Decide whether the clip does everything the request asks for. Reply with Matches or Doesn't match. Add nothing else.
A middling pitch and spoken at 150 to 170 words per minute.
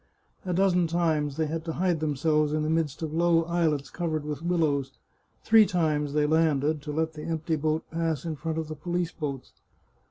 Doesn't match